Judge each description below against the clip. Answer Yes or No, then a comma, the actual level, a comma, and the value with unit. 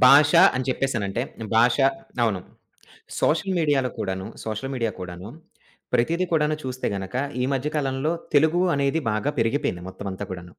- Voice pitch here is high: No, low, 130 Hz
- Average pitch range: No, wide, 6.2 semitones